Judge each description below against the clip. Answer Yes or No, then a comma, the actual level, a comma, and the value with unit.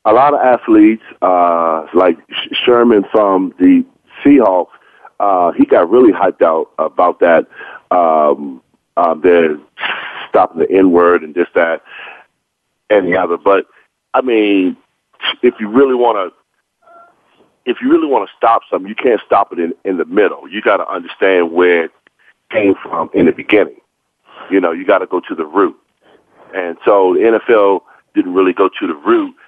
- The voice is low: Yes, low, 125 Hz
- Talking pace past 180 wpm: No, average, 175 wpm